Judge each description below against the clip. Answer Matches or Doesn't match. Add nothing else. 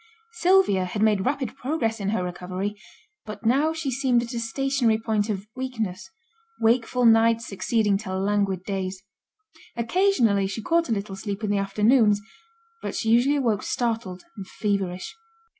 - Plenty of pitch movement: Doesn't match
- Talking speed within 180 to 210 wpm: Doesn't match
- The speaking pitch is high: Matches